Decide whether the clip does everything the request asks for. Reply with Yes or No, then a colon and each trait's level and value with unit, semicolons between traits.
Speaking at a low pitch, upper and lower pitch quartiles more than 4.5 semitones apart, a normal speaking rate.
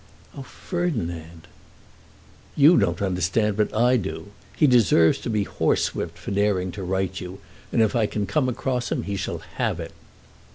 Yes: low, 100 Hz; average, 5.1 semitones; average, 170 wpm